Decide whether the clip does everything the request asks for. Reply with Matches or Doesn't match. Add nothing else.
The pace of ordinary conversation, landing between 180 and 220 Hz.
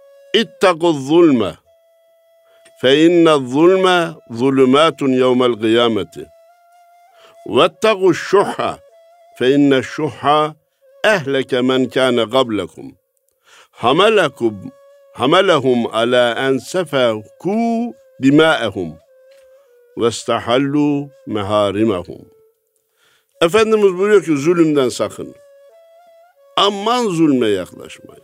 Doesn't match